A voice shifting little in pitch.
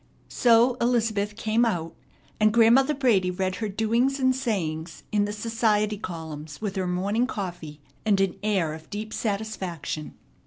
No: average, 4.0 semitones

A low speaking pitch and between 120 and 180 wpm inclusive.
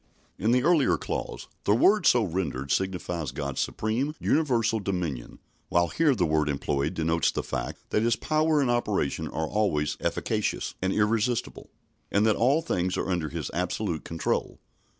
Yes: low, 100 Hz; average, 160 wpm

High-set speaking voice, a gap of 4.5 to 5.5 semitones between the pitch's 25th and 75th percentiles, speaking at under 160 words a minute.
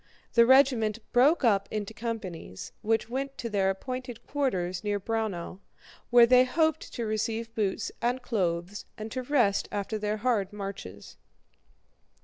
No: high, 220 Hz; average, 3.8 semitones; average, 140 wpm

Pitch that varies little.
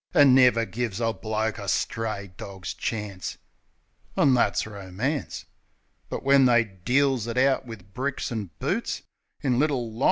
No: average, 3.8 semitones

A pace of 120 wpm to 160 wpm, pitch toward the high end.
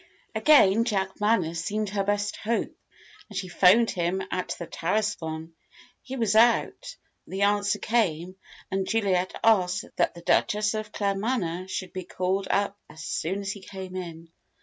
Yes: average, 155 wpm; high, 195 Hz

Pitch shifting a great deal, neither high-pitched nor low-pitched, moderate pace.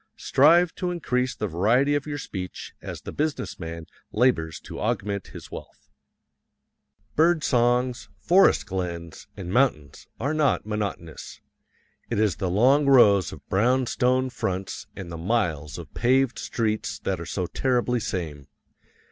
No: wide, 6.1 semitones; low, 110 Hz; average, 145 wpm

